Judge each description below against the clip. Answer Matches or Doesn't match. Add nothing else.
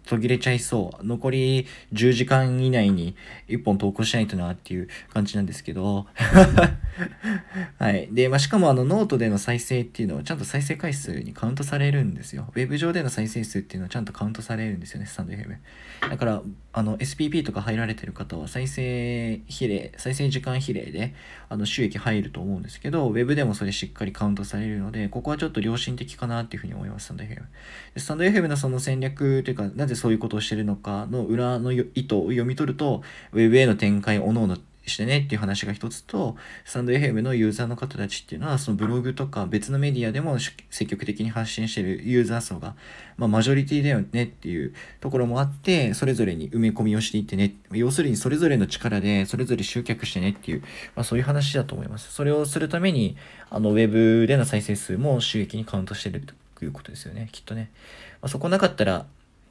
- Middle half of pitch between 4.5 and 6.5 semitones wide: Doesn't match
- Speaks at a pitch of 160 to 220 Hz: Doesn't match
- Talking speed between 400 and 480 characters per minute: Matches